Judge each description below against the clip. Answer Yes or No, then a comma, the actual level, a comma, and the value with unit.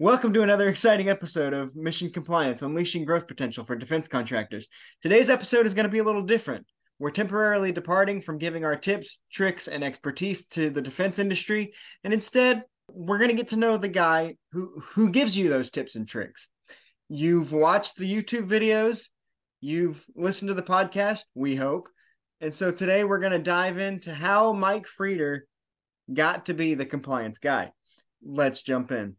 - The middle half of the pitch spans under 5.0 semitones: No, average, 5.3 semitones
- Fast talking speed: No, average, 180 wpm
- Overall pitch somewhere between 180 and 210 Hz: Yes, medium, 185 Hz